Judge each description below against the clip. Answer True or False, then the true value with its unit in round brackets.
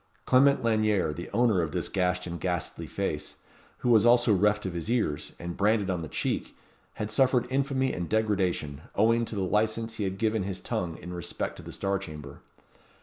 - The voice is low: True (100 Hz)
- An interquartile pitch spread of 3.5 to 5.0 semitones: True (4.2 semitones)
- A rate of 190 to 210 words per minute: True (195 wpm)